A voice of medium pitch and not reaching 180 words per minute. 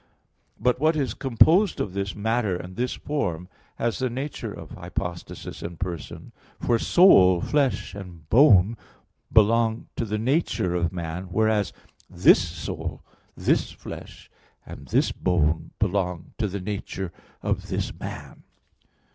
No: low, 100 Hz; slow, 135 wpm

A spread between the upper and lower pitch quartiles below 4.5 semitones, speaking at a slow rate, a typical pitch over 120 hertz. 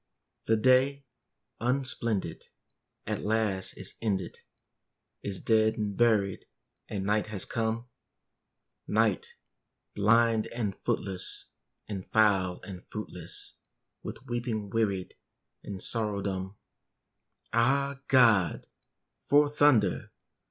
No: average, 3.2 semitones; slow, 95 wpm; low, 110 Hz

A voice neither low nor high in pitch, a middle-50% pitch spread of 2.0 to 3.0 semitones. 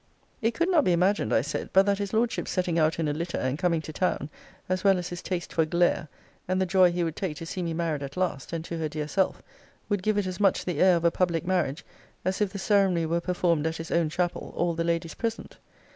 Yes: medium, 175 Hz; narrow, 2.4 semitones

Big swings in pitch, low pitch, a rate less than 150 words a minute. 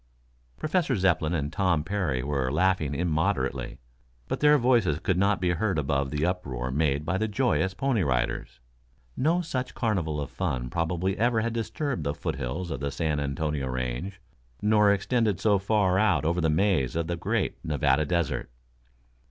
No: wide, 6.1 semitones; very low, 85 Hz; average, 165 wpm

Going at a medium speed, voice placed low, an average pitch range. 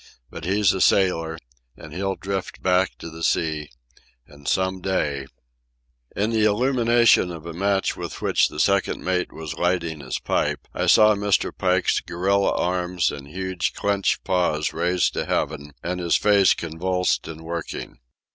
Yes: average, 160 wpm; very low, 90 Hz; average, 3.2 semitones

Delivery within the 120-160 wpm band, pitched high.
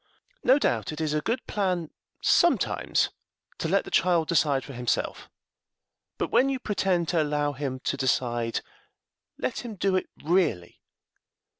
No: average, 150 wpm; medium, 160 Hz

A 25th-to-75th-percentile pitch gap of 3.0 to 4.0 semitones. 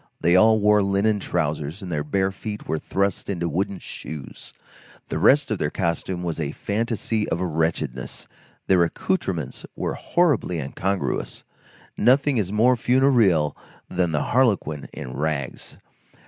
No: wide, 5.4 semitones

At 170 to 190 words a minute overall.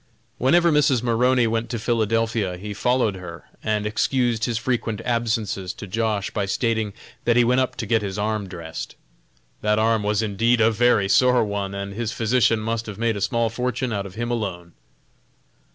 Yes: average, 185 wpm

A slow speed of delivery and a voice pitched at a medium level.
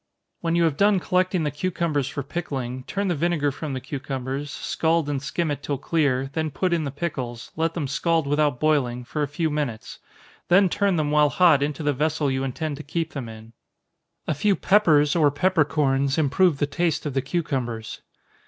No: average, 195 wpm; medium, 150 Hz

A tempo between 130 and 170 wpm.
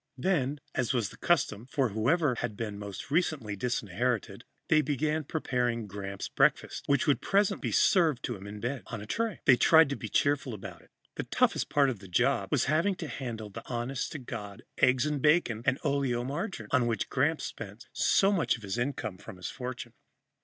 No: average, 195 wpm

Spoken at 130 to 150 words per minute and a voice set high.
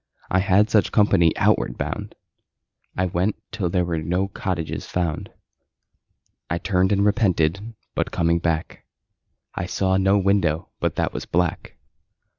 No: average, 140 wpm; very low, 90 Hz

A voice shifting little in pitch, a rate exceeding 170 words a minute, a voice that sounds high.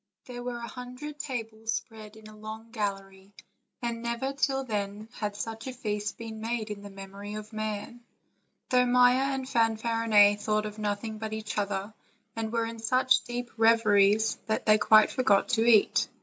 Yes: narrow, 2.3 semitones; average, 180 wpm; high, 220 Hz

